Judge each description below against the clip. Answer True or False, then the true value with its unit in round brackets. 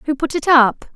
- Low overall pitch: False (280 Hz)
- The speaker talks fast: True (250 wpm)